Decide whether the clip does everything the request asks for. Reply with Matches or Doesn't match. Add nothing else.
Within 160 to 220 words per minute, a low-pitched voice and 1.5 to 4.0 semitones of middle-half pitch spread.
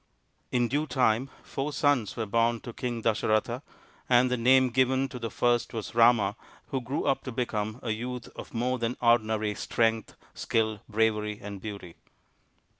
Matches